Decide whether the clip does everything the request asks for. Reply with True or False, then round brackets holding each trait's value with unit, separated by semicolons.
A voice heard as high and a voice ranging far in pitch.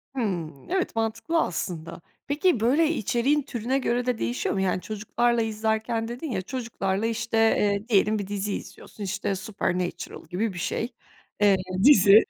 False (220 Hz; 3.5 semitones)